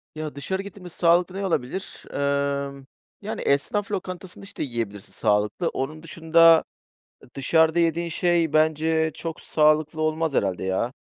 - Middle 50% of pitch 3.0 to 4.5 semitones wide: Yes, average, 3.5 semitones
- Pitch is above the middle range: No, medium, 160 Hz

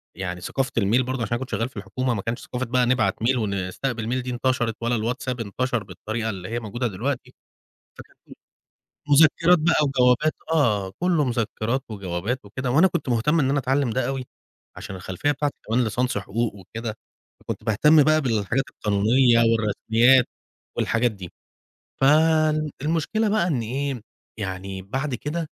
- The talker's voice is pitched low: Yes, low, 125 Hz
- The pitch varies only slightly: No, average, 3.9 semitones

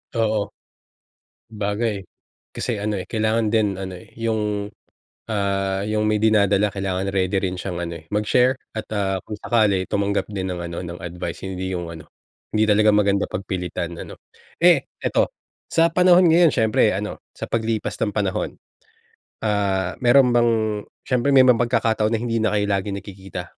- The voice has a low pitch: Yes, low, 105 Hz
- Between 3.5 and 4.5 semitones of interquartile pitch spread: No, average, 2.7 semitones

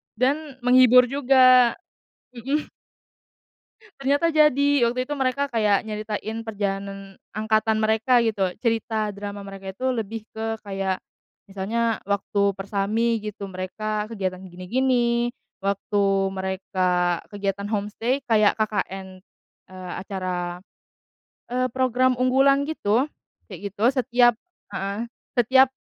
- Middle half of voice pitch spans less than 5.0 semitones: Yes, average, 4.2 semitones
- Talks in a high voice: Yes, high, 215 Hz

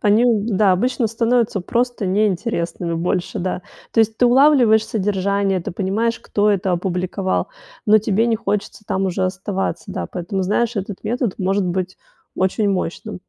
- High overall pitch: Yes, high, 200 Hz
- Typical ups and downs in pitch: Yes, average, 3.2 semitones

